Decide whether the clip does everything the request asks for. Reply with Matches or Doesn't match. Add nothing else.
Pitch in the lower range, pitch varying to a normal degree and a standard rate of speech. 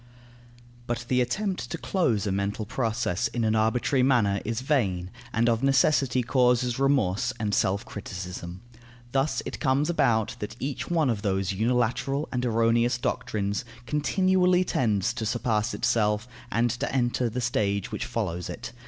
Matches